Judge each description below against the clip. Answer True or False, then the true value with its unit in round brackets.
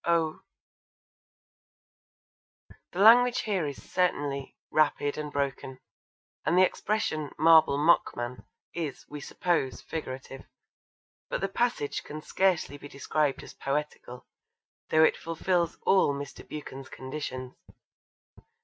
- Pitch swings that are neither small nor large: True (3.6 semitones)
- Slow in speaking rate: True (110 wpm)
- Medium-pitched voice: True (150 Hz)